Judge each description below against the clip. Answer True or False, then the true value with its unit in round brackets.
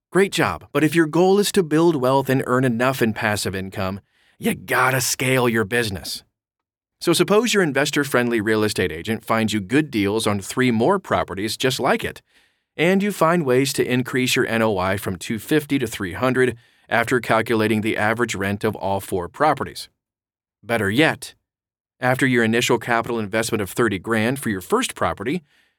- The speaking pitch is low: True (120 Hz)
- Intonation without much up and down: False (3.8 semitones)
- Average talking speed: True (175 wpm)